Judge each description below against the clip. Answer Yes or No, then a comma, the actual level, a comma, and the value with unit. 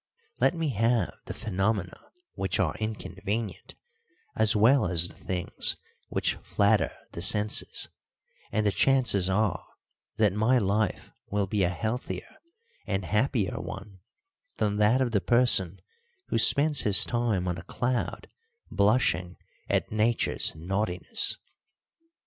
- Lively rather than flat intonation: No, average, 3.6 semitones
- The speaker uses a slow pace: Yes, slow, 125 wpm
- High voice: No, low, 105 Hz